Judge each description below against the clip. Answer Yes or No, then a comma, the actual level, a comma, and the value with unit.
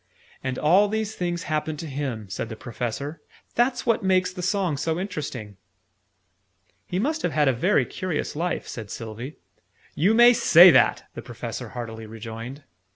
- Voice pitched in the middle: Yes, medium, 155 Hz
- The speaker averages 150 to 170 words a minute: Yes, average, 160 wpm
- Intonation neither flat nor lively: No, wide, 7.3 semitones